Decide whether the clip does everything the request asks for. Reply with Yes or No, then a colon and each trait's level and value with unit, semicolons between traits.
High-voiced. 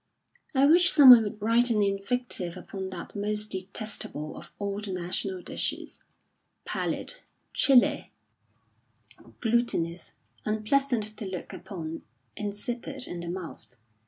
Yes: high, 210 Hz